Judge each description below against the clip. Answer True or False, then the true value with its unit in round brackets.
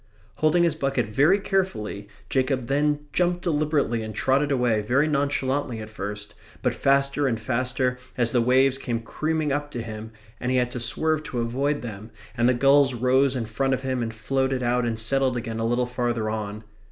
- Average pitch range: True (3.3 semitones)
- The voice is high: False (130 Hz)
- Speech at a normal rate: True (190 wpm)